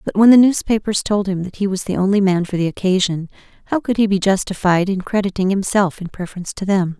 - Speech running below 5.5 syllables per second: No, 6.2 syllables/s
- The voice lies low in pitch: No, high, 195 Hz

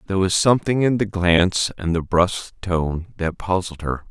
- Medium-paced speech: Yes, average, 190 wpm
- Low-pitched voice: Yes, very low, 90 Hz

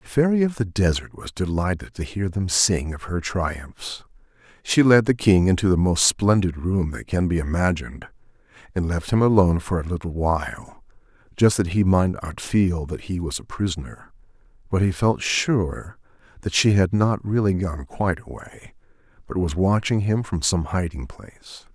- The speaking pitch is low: Yes, very low, 95 Hz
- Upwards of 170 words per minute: Yes, average, 180 wpm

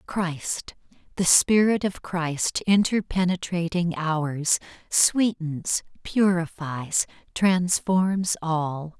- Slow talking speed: Yes, slow, 75 wpm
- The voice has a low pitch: No, medium, 175 Hz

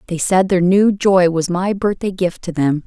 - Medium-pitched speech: Yes, medium, 180 Hz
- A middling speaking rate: No, fast, 230 wpm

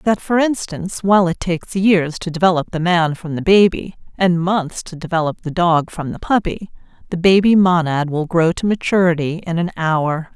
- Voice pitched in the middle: Yes, medium, 175 Hz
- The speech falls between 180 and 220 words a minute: Yes, average, 190 wpm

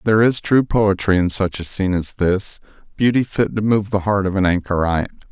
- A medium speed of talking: No, fast, 215 wpm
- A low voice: Yes, low, 100 Hz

